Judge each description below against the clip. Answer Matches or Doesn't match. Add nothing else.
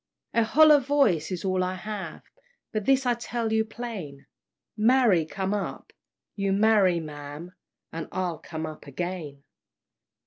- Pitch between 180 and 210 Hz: Matches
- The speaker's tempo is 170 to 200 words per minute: Doesn't match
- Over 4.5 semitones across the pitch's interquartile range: Matches